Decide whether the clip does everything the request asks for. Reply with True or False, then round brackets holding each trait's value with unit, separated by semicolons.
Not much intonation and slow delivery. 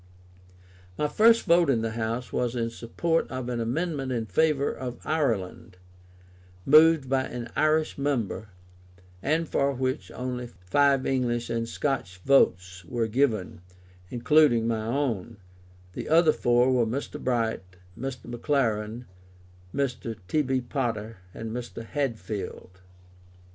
False (3.7 semitones; 125 wpm)